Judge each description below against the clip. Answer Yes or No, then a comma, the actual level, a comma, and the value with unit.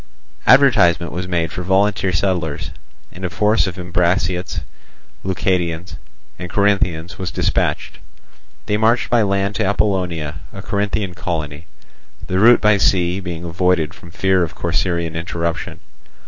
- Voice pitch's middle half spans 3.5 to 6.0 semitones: No, narrow, 2.6 semitones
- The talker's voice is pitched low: Yes, very low, 90 Hz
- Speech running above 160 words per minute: No, slow, 135 wpm